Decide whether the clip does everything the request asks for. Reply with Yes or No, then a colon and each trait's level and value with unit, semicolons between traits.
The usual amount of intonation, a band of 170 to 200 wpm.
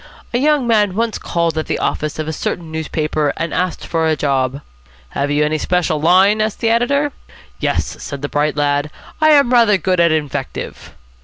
No: wide, 6.2 semitones; average, 190 wpm